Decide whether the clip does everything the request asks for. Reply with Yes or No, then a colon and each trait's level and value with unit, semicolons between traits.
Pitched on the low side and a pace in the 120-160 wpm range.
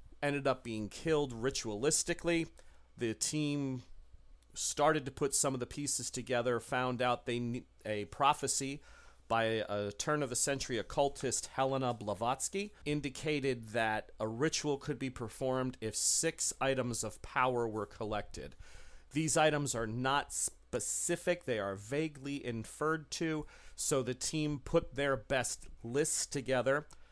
Yes: low, 130 Hz; slow, 135 wpm